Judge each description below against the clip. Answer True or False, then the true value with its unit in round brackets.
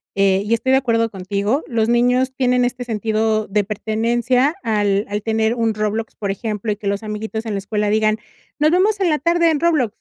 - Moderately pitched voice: False (225 Hz)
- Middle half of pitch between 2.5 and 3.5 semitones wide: True (3.0 semitones)